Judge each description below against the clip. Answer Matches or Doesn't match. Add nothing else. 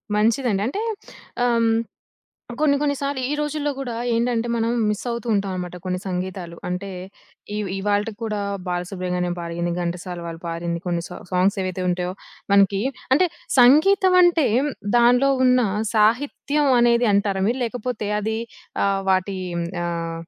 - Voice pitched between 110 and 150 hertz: Doesn't match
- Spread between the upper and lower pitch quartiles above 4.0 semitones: Matches